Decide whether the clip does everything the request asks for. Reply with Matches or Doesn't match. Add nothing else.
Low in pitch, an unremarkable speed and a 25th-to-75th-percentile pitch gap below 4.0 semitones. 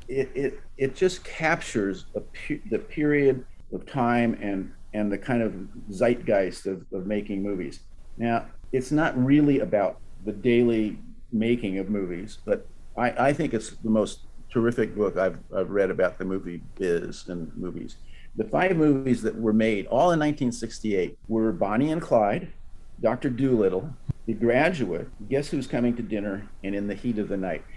Doesn't match